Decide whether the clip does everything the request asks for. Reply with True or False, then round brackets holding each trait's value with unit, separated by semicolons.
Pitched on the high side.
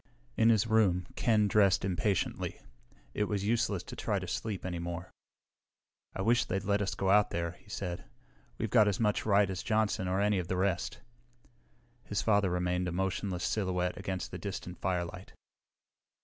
False (95 Hz)